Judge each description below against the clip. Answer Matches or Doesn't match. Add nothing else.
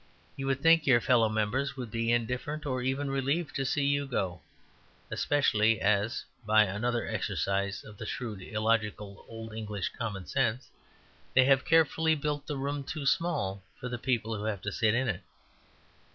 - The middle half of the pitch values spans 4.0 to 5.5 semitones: Matches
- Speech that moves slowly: Doesn't match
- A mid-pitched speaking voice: Doesn't match